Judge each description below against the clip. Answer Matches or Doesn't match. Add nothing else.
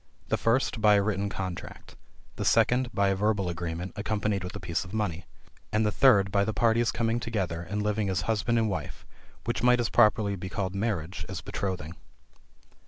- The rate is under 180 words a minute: Doesn't match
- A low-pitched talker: Matches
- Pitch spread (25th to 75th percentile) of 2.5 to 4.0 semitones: Matches